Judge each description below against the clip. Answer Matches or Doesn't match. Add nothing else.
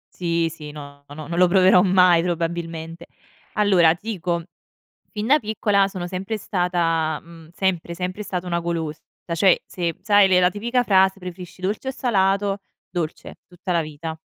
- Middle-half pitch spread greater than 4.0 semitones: Doesn't match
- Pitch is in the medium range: Matches